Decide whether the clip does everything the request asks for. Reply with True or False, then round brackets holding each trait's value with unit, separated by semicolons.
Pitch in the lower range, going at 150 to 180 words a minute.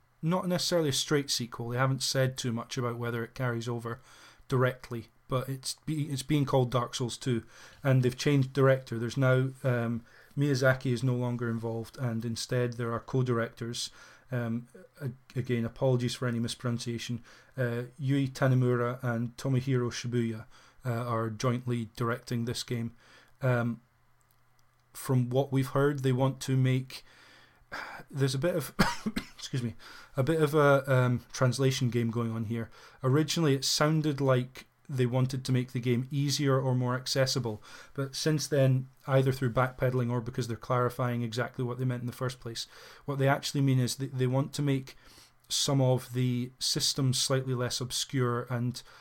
True (125 Hz; 165 wpm)